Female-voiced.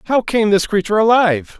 No: male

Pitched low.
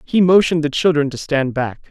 No: medium, 155 Hz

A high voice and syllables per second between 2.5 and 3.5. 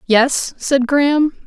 Yes: very high, 270 Hz; 3.2 syllables/s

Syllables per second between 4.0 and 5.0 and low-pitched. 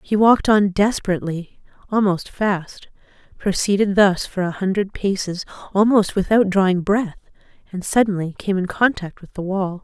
No: 4.9 syllables/s; high, 195 Hz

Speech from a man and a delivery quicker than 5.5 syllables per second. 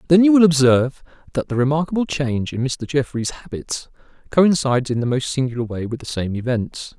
Yes: male; 5.8 syllables/s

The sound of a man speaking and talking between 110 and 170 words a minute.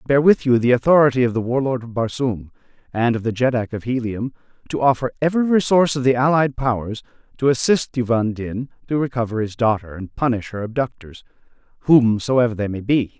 No: male; average, 180 wpm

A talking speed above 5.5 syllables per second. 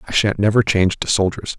Yes: 6.3 syllables/s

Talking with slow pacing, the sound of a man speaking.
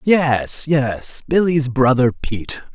Yes: slow, 110 wpm; male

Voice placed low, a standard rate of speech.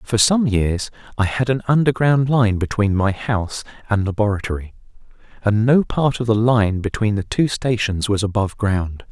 Yes: low, 110 Hz; average, 170 wpm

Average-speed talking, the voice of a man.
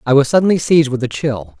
No: fast, 265 wpm; male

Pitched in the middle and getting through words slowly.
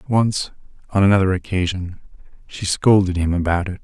No: very low, 95 Hz; slow, 110 wpm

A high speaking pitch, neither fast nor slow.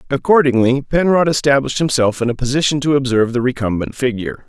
No: low, 130 Hz; average, 160 wpm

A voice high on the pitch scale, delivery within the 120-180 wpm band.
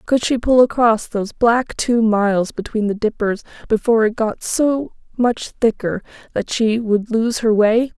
Yes: high, 225 Hz; average, 175 wpm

